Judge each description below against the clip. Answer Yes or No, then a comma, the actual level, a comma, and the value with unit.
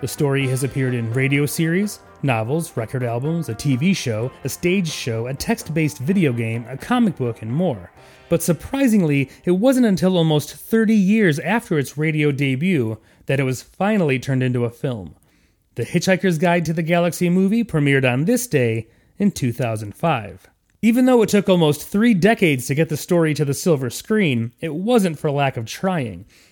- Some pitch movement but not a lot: No, wide, 6.4 semitones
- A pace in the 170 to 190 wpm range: Yes, average, 180 wpm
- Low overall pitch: No, medium, 155 Hz